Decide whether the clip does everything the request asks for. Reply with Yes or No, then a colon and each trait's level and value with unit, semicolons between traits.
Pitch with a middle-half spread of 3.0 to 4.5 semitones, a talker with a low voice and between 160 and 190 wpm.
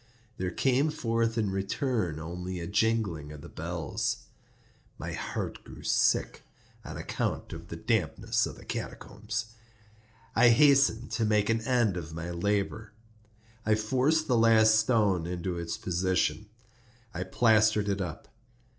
No: average, 4.2 semitones; low, 105 Hz; slow, 135 wpm